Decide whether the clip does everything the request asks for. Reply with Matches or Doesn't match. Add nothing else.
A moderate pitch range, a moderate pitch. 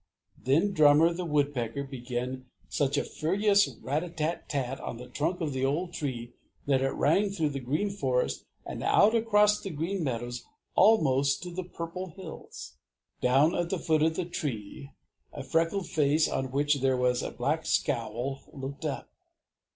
Matches